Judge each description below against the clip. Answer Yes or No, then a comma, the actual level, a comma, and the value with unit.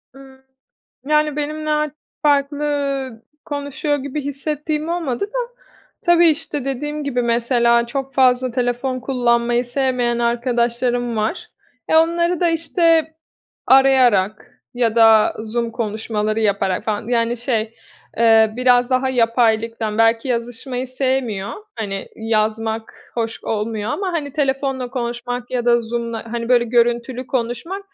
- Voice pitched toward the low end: No, high, 245 Hz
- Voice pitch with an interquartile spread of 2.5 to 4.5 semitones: Yes, average, 3.4 semitones